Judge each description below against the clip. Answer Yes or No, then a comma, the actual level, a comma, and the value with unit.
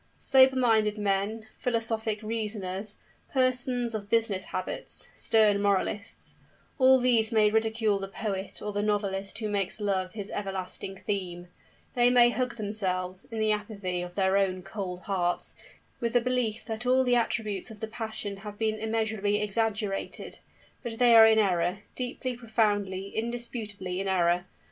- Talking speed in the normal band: Yes, average, 150 wpm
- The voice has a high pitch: Yes, high, 210 Hz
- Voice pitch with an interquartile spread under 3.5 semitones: Yes, average, 2.7 semitones